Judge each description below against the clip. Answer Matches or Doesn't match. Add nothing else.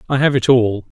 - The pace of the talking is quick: Matches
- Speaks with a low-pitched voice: Matches